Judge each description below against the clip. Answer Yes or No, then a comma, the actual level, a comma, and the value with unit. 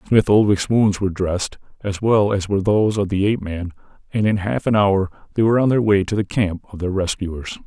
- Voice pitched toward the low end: Yes, low, 100 Hz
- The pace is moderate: No, fast, 235 wpm